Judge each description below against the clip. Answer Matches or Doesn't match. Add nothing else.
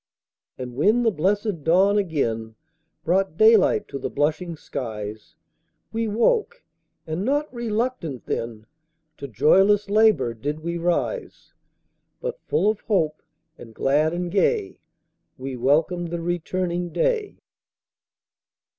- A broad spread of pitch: Matches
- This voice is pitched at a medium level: Matches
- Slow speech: Matches